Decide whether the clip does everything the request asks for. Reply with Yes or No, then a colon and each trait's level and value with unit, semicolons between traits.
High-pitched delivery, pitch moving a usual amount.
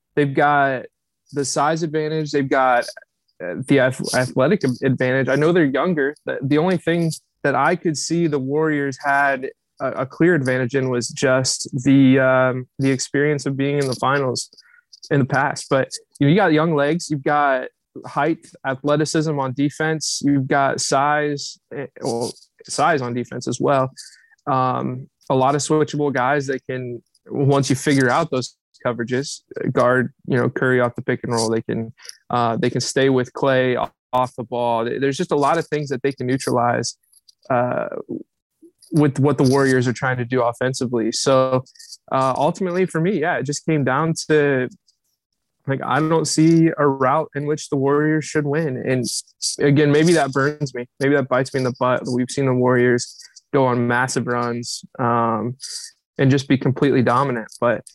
No: medium, 140 Hz; average, 3.0 semitones